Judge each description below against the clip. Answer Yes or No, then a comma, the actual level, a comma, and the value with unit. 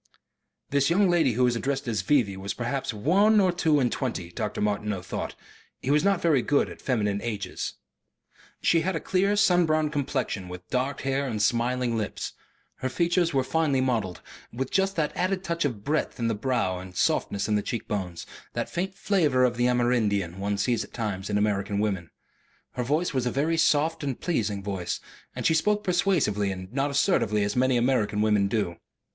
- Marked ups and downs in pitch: Yes, wide, 7.0 semitones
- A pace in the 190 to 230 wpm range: Yes, average, 195 wpm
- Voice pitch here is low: Yes, low, 125 Hz